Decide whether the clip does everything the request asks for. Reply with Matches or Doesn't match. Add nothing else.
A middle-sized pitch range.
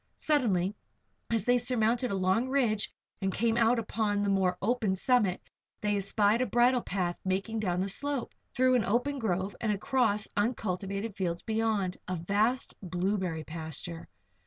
Matches